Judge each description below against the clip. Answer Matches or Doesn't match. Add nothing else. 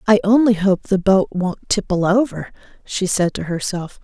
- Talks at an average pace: Matches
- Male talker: Doesn't match